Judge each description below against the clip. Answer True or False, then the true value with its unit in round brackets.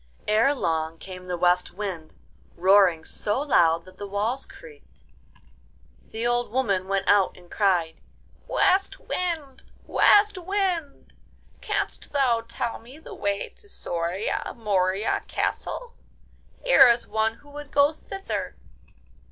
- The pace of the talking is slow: True (125 wpm)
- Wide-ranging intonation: True (7.7 semitones)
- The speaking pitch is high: True (220 Hz)